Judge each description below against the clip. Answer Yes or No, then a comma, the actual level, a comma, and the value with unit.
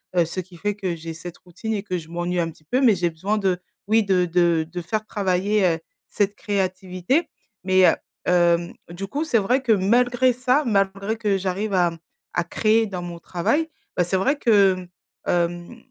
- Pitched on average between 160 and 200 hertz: Yes, high, 190 Hz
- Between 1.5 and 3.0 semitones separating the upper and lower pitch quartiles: No, average, 3.7 semitones